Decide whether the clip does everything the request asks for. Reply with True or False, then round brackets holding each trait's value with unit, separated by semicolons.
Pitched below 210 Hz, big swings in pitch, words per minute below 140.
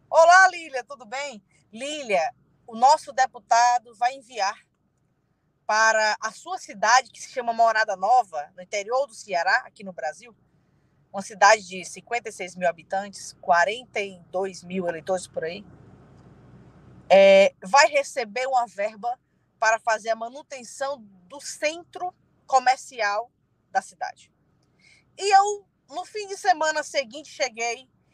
False (235 Hz; 6.5 semitones; 125 wpm)